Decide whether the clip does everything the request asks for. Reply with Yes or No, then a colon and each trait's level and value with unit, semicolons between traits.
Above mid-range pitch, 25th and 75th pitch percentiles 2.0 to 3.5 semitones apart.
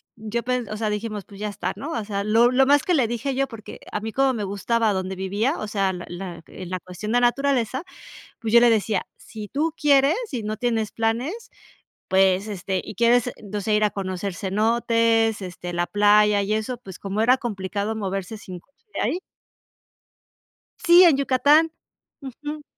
No: high, 220 Hz; average, 3.9 semitones